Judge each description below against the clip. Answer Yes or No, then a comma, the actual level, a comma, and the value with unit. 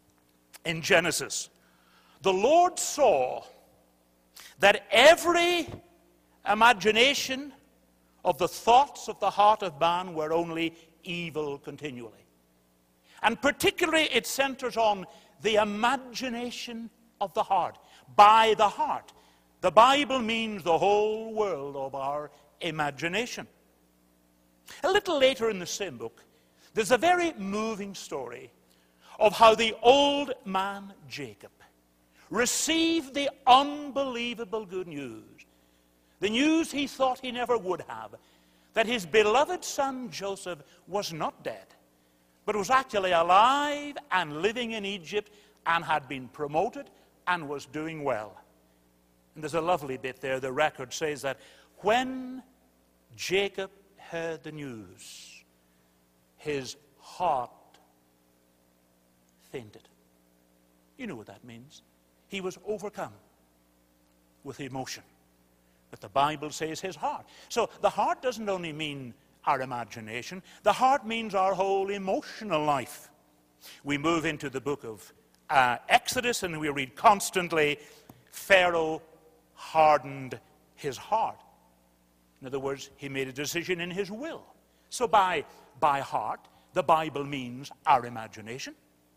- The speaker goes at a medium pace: No, slow, 120 wpm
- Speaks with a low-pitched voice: No, medium, 165 Hz